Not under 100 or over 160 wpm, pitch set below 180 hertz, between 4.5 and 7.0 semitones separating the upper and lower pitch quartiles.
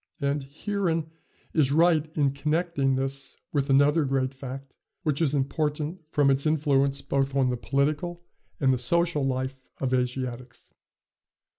No: average, 140 wpm; medium, 140 Hz; narrow, 2.5 semitones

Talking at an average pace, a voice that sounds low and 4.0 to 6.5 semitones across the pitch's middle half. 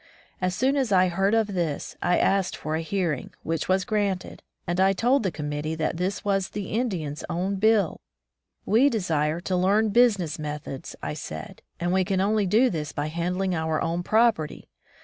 No: average, 185 wpm; medium, 185 Hz; average, 4.3 semitones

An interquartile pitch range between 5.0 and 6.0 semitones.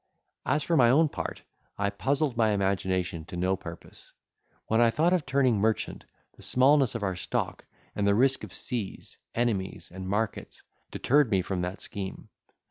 Yes: wide, 5.6 semitones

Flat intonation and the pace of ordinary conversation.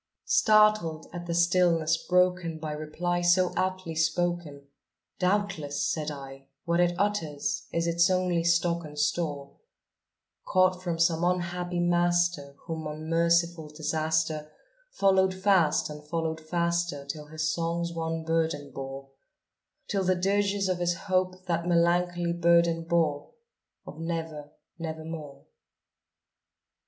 No: narrow, 2.1 semitones; slow, 120 wpm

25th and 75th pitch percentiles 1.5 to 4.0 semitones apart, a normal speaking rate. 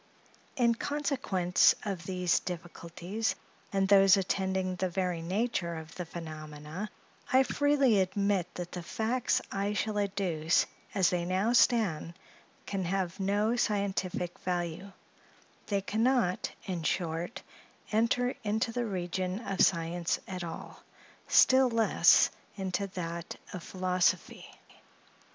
No: average, 3.3 semitones; slow, 120 wpm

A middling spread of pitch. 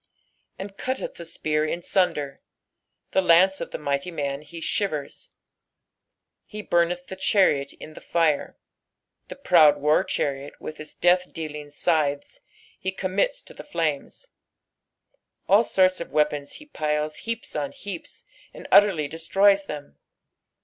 Yes: average, 4.2 semitones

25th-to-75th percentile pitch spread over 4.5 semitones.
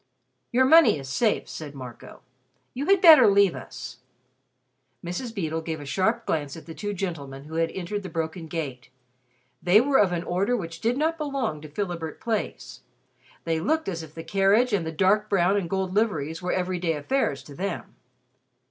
Yes: average, 5.0 semitones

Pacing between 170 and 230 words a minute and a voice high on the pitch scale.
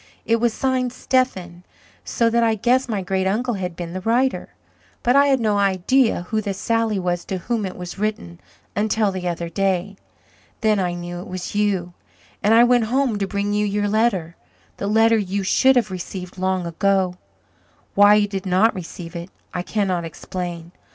Yes: average, 185 wpm; high, 200 Hz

